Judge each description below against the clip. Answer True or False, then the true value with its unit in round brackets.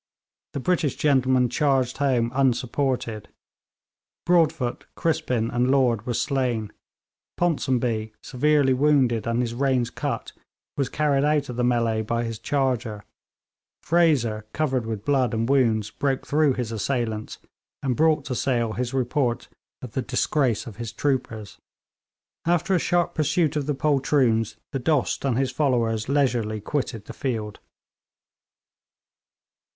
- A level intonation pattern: False (3.5 semitones)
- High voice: False (130 Hz)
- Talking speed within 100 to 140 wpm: True (135 wpm)